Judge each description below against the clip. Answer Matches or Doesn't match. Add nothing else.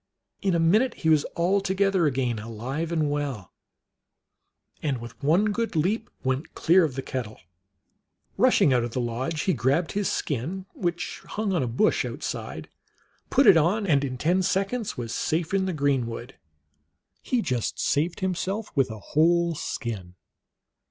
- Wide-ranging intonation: Matches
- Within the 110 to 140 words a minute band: Doesn't match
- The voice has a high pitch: Doesn't match